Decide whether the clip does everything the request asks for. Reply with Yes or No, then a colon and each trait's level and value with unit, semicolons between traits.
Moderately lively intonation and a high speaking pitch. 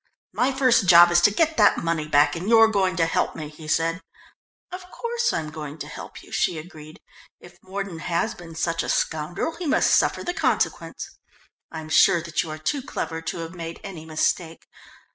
No: average, 4.3 semitones; medium, 170 Hz